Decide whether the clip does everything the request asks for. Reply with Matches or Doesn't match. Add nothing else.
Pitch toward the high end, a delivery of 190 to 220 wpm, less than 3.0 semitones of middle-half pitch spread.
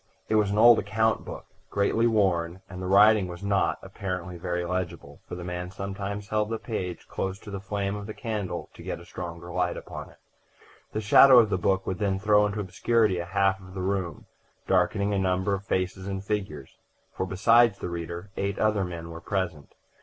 Doesn't match